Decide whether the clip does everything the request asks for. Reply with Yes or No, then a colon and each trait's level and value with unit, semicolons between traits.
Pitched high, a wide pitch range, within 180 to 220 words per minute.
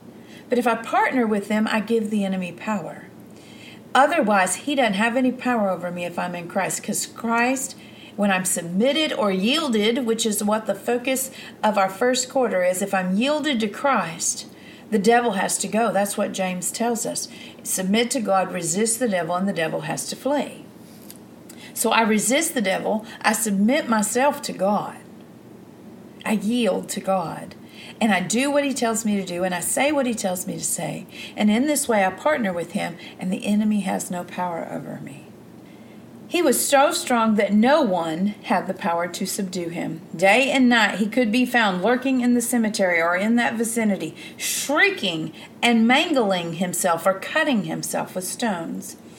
No: high, 220 Hz; average, 4.5 semitones; average, 185 wpm